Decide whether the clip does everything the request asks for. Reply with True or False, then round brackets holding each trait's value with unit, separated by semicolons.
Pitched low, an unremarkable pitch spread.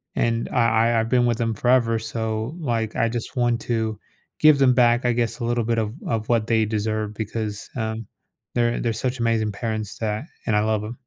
False (115 Hz; 1.5 semitones)